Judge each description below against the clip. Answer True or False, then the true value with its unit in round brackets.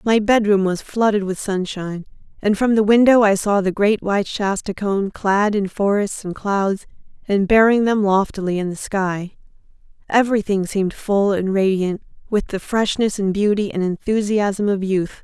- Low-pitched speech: False (200 Hz)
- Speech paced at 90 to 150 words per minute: False (170 wpm)